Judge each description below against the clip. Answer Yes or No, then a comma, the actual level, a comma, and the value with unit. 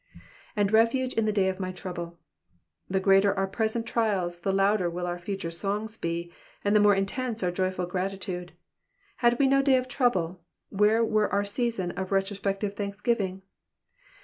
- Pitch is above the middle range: Yes, high, 195 Hz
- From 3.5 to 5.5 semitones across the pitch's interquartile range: No, average, 2.9 semitones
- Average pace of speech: Yes, average, 170 wpm